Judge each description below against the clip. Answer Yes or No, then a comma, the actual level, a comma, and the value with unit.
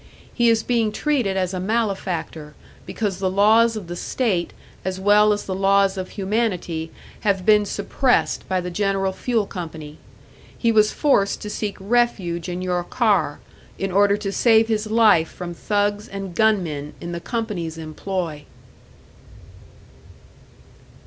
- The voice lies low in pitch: No, high, 195 Hz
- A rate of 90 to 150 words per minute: Yes, average, 145 wpm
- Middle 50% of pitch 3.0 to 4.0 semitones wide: Yes, average, 3.3 semitones